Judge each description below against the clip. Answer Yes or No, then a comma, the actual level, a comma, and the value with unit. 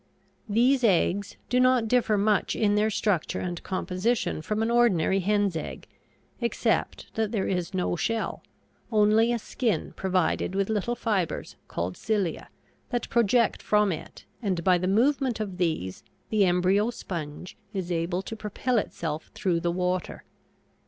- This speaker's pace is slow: No, average, 150 wpm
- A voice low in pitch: No, high, 200 Hz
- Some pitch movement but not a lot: Yes, average, 3.8 semitones